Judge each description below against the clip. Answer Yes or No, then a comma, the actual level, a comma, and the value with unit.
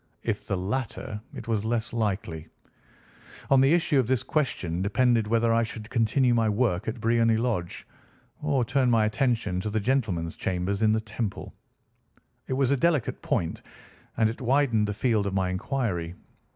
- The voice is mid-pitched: No, low, 115 Hz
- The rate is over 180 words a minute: No, average, 170 wpm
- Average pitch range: Yes, average, 3.8 semitones